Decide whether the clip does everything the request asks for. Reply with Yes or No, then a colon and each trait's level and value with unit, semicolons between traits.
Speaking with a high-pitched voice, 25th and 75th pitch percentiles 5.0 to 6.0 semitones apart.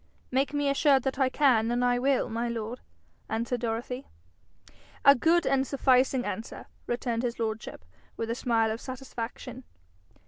No: high, 245 Hz; narrow, 2.6 semitones